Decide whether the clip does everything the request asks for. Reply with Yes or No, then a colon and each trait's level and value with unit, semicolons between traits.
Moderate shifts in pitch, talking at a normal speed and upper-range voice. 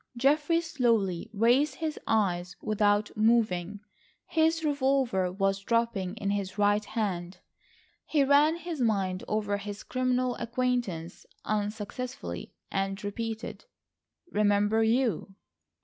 No: average, 4.2 semitones; slow, 100 wpm; high, 215 Hz